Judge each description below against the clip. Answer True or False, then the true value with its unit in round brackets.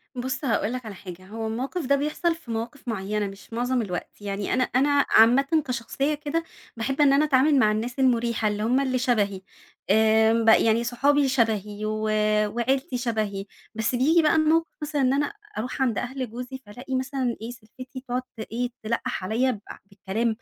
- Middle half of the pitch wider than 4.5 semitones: False (3.6 semitones)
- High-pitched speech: True (245 Hz)